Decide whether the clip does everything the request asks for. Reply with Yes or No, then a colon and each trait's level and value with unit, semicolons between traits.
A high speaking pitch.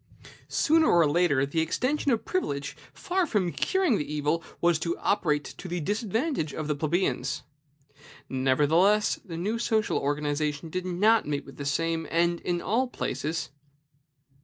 No: medium, 170 Hz